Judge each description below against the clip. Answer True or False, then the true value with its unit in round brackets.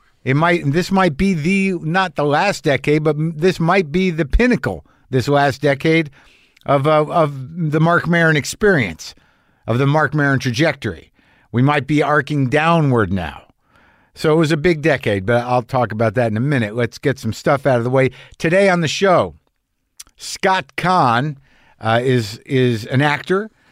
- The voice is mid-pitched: True (145 Hz)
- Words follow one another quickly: False (175 wpm)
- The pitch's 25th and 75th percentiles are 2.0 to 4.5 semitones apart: False (5.2 semitones)